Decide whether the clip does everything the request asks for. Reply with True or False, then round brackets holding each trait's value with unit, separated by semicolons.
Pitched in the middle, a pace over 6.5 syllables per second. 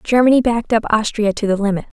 False (220 Hz; 6.7 syllables/s)